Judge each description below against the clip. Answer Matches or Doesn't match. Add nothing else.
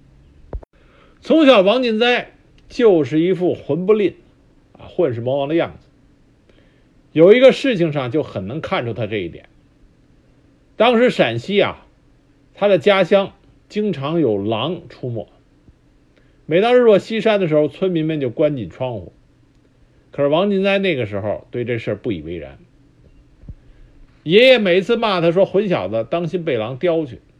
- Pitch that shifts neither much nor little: Doesn't match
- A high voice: Doesn't match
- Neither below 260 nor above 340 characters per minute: Doesn't match